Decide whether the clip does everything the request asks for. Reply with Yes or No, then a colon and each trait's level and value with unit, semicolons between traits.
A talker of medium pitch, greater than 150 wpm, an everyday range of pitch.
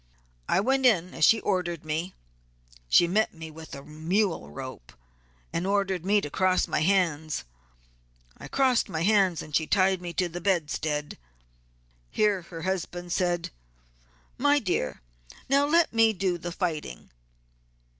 No: medium, 180 Hz; average, 145 wpm; average, 3.8 semitones